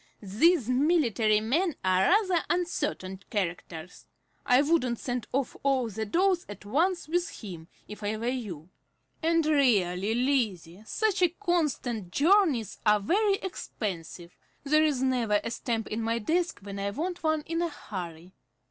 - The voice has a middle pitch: No, high, 245 Hz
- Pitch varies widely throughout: Yes, wide, 8.2 semitones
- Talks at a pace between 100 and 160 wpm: Yes, average, 150 wpm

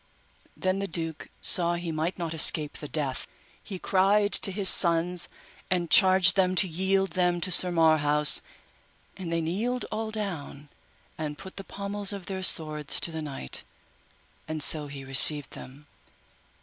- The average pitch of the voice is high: No, medium, 175 Hz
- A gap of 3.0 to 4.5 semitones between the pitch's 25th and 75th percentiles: Yes, average, 3.6 semitones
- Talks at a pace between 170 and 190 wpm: No, average, 160 wpm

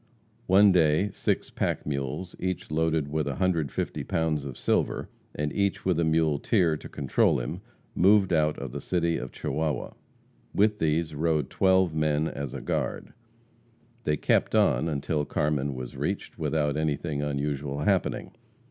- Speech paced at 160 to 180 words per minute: No, average, 150 wpm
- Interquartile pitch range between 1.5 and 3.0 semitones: Yes, average, 2.7 semitones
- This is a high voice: No, very low, 75 Hz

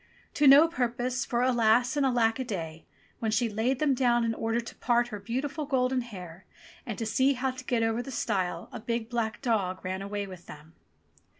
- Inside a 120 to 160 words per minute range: No, fast, 205 wpm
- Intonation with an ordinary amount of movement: Yes, average, 3.3 semitones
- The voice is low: No, high, 235 Hz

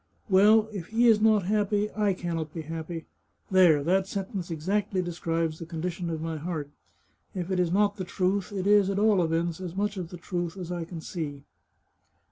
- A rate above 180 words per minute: Yes, fast, 205 wpm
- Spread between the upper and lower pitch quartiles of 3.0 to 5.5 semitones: Yes, average, 3.4 semitones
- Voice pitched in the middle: Yes, medium, 180 Hz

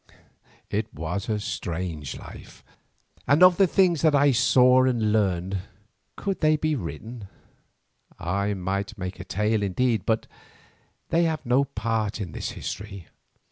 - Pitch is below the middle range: Yes, low, 110 Hz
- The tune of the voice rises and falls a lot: Yes, wide, 6.1 semitones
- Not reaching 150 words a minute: Yes, average, 140 wpm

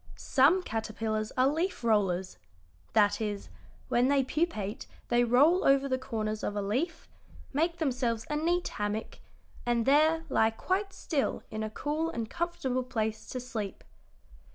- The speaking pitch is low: No, very high, 250 Hz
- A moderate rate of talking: Yes, average, 150 wpm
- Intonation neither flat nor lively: No, wide, 5.9 semitones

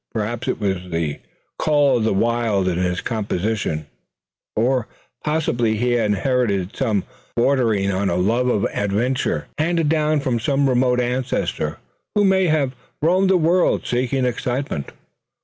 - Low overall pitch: Yes, low, 120 Hz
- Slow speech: No, average, 150 wpm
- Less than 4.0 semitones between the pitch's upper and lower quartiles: No, average, 5.2 semitones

